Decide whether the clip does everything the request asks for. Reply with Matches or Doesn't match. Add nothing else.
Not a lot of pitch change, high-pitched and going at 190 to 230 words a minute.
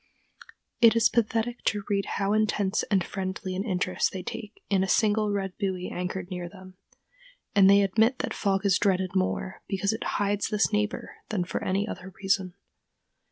Doesn't match